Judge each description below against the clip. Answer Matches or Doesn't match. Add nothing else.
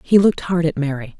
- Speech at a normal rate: Doesn't match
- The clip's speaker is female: Matches